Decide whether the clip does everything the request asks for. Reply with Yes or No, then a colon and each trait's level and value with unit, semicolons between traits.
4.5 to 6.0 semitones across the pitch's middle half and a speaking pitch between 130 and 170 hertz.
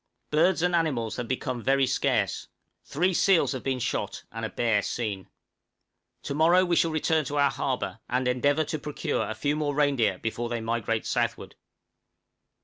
Yes: average, 5.0 semitones; low, 135 Hz